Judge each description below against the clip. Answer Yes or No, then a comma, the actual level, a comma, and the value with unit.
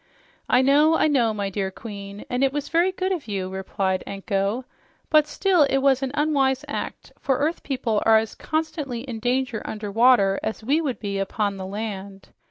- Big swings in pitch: Yes, wide, 5.8 semitones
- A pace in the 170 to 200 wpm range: Yes, average, 190 wpm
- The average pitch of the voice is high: Yes, high, 240 Hz